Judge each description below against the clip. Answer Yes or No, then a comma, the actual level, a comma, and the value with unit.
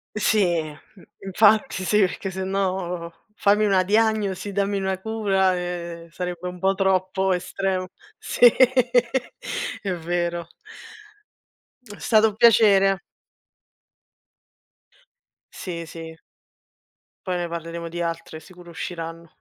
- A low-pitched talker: No, medium, 185 Hz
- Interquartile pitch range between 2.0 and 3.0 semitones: Yes, narrow, 2.4 semitones